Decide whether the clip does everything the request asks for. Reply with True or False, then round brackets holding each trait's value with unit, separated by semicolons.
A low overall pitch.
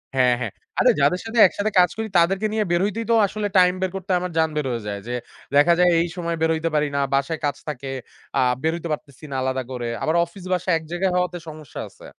False (170 Hz)